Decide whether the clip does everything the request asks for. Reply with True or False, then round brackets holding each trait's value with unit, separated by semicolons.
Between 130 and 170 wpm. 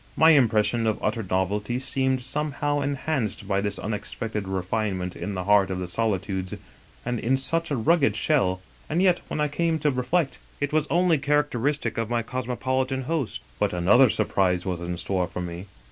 False (180 wpm)